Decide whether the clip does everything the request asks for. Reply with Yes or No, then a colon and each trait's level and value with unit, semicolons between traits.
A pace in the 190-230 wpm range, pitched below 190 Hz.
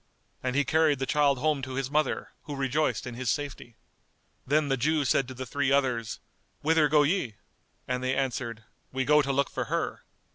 Yes: average, 195 wpm; low, 135 Hz